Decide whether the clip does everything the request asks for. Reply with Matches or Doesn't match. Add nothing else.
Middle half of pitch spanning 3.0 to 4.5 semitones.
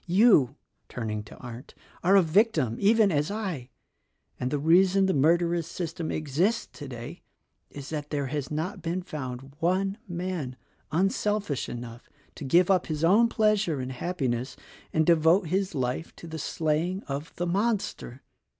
Doesn't match